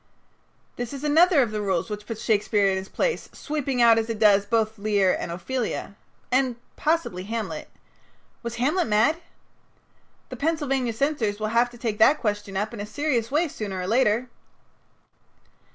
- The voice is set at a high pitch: Yes, high, 230 Hz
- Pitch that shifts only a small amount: No, average, 4.5 semitones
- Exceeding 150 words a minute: Yes, average, 170 wpm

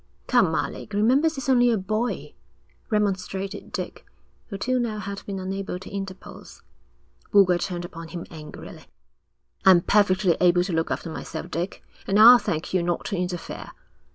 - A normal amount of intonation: Yes, average, 3.1 semitones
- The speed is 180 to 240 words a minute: No, average, 155 wpm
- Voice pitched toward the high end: Yes, high, 195 Hz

